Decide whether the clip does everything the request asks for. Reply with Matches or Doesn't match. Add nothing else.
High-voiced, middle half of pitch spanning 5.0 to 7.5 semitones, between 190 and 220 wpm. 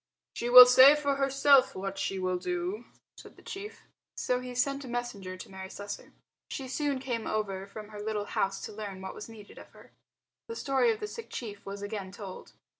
Matches